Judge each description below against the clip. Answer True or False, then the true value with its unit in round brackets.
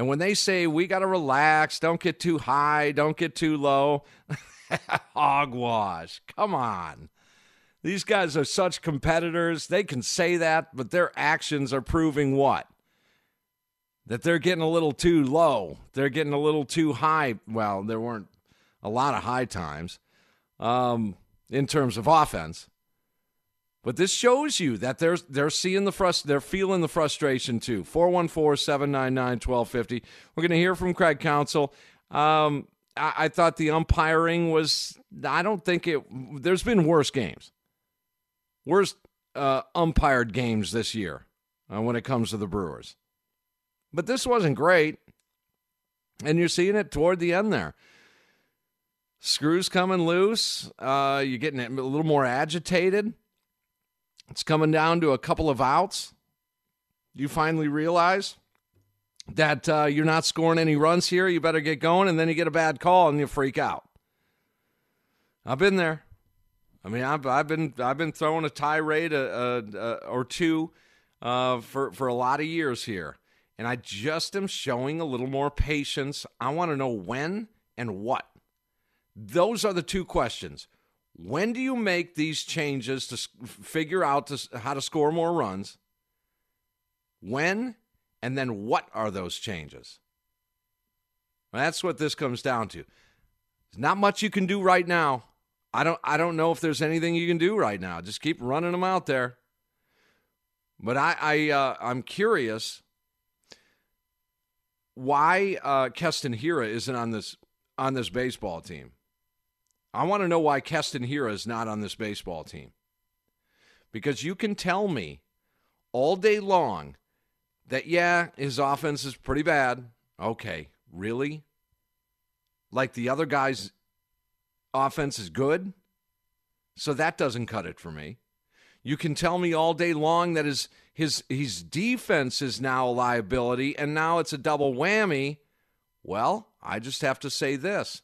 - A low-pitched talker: False (145 Hz)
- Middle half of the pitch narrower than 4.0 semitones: False (5.4 semitones)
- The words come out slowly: False (155 wpm)